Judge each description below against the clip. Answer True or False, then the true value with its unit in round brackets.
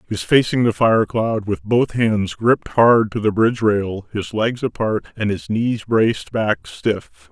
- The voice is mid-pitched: False (110 Hz)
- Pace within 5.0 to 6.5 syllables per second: False (4.2 syllables/s)